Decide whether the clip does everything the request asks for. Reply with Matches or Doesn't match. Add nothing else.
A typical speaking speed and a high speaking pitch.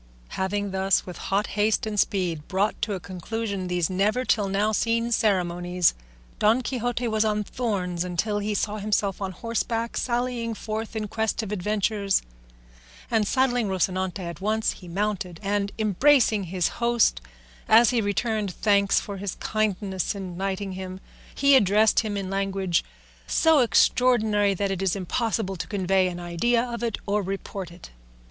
Matches